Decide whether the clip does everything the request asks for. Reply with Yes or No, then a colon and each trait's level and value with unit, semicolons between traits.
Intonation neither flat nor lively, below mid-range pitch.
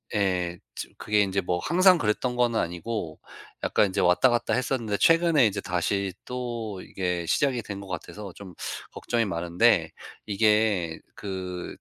Yes: average, 4.7 semitones; low, 100 Hz